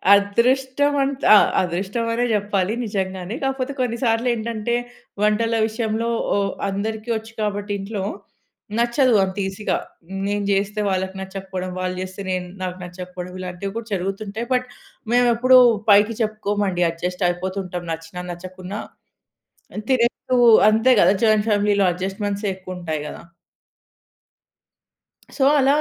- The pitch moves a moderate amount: Yes, average, 3.6 semitones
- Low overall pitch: No, high, 205 Hz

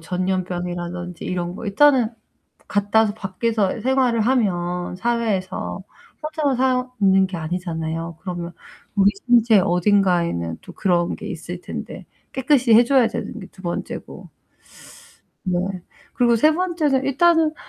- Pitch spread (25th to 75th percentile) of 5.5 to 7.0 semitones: Yes, wide, 5.9 semitones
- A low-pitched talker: No, high, 200 Hz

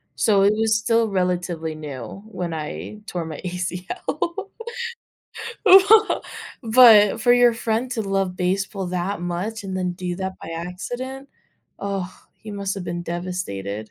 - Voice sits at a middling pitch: No, high, 195 Hz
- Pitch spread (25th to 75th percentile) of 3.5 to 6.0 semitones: Yes, average, 3.9 semitones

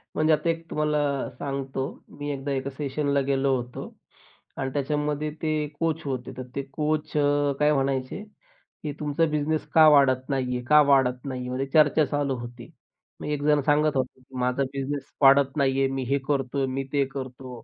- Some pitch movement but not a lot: No, narrow, 2.0 semitones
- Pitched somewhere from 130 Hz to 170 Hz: Yes, medium, 140 Hz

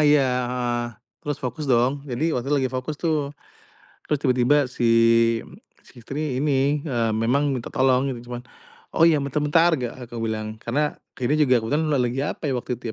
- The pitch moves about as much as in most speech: Yes, average, 3.3 semitones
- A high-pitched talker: No, low, 130 Hz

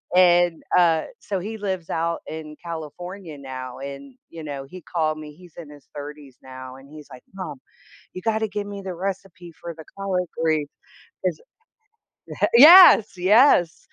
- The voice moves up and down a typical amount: Yes, average, 4.2 semitones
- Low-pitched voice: No, medium, 170 Hz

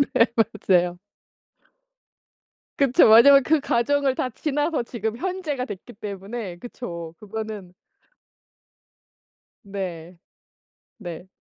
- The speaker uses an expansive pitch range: Yes, wide, 6.0 semitones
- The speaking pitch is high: Yes, high, 220 Hz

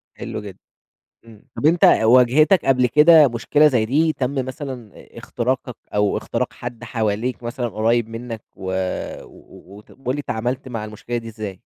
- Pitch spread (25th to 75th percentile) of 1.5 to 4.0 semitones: Yes, average, 3.3 semitones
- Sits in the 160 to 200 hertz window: No, low, 120 Hz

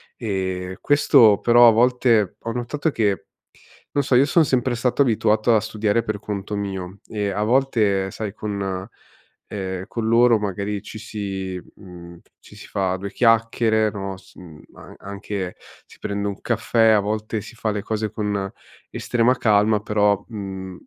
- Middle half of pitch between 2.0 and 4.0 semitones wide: Yes, average, 2.7 semitones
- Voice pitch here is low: Yes, low, 105 Hz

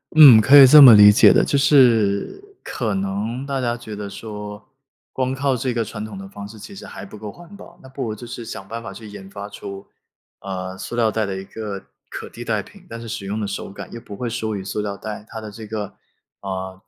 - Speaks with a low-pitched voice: Yes, low, 110 Hz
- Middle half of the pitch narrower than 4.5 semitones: Yes, average, 3.2 semitones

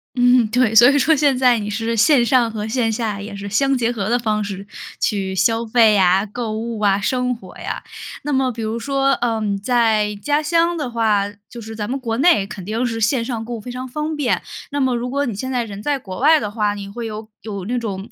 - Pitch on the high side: Yes, high, 230 Hz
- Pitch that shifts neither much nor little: Yes, average, 3.2 semitones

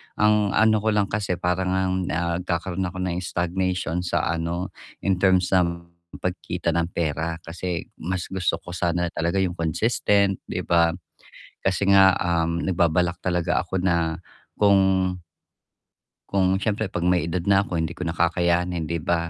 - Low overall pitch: Yes, very low, 90 Hz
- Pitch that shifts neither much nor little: No, narrow, 1.8 semitones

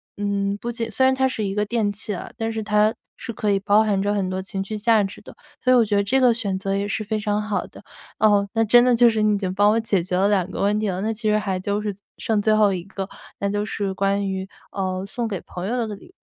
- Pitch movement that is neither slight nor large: No, narrow, 1.8 semitones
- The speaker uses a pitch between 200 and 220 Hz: Yes, high, 205 Hz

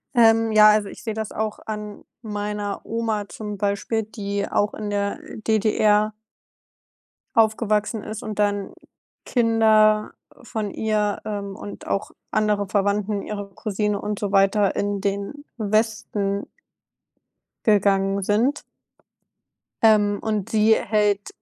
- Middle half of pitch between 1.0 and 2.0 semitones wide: Yes, narrow, 1.3 semitones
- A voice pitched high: Yes, high, 210 Hz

